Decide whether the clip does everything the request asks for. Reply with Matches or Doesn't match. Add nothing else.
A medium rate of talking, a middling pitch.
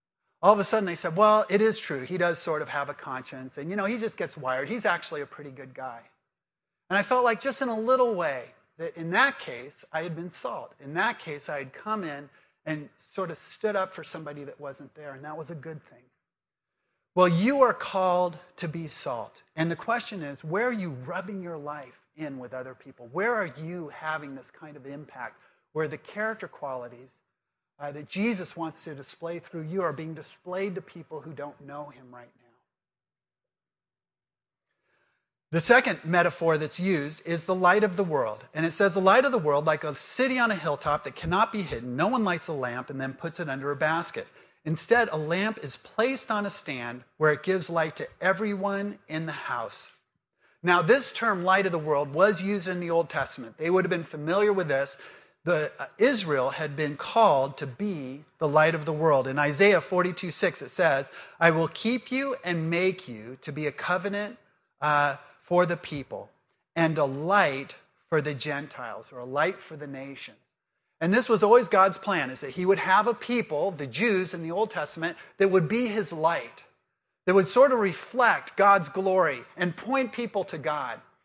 Doesn't match